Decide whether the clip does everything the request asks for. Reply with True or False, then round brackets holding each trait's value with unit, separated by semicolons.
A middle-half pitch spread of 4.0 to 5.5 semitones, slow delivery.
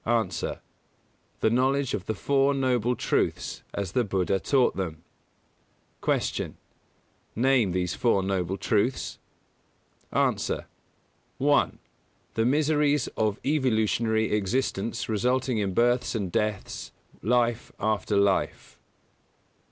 True (4.4 semitones; 110 wpm)